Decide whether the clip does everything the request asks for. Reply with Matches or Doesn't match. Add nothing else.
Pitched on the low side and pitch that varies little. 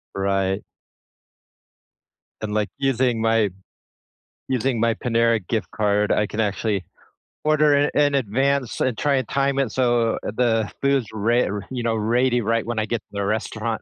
Doesn't match